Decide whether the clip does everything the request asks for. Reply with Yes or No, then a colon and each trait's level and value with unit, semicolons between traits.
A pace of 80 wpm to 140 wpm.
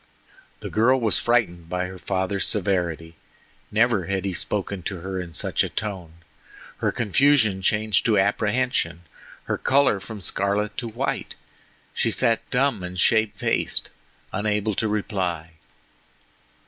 Yes: slow, 135 wpm